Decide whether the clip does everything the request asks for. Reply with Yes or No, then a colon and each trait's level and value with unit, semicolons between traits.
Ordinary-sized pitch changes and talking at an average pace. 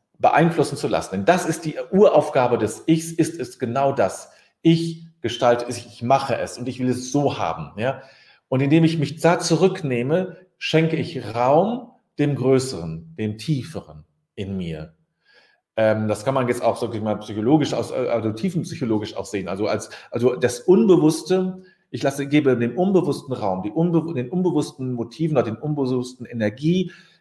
No: wide, 6.1 semitones; average, 170 wpm